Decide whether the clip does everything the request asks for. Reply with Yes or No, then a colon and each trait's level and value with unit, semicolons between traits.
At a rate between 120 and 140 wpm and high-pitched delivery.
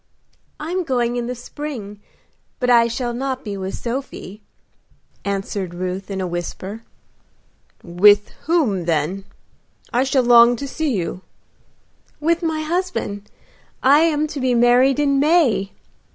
Yes: slow, 135 wpm; high, 240 Hz